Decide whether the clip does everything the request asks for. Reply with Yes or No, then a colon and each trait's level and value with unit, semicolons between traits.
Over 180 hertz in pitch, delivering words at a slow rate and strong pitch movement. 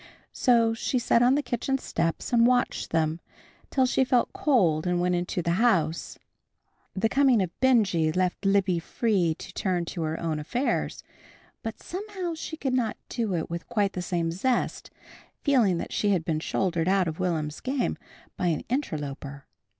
No: high, 190 Hz; average, 175 wpm; wide, 6.7 semitones